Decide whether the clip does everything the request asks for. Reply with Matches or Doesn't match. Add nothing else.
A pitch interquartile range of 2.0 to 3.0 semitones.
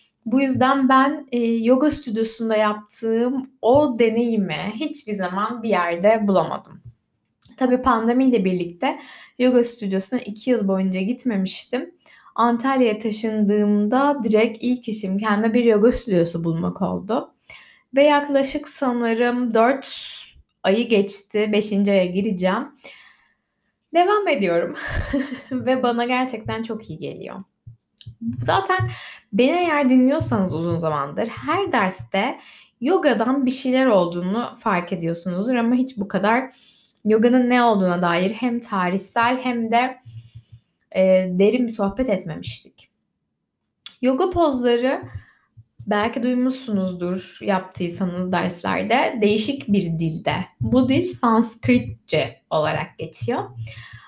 Doesn't match